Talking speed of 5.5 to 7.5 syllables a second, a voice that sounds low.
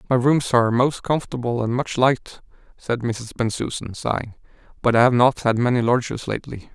Yes: 5.6 syllables/s; low, 120 Hz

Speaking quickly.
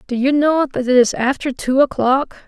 Yes: fast, 220 wpm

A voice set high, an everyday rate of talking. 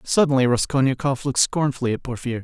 No: low, 130 Hz; average, 150 wpm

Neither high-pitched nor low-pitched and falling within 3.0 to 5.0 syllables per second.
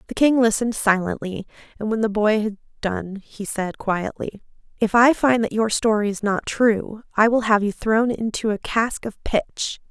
No: high, 215 Hz; 4.8 syllables/s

